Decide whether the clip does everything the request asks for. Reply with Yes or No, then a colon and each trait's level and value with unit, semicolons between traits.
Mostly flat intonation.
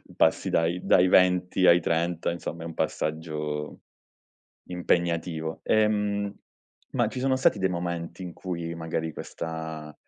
Yes: narrow, 1.9 semitones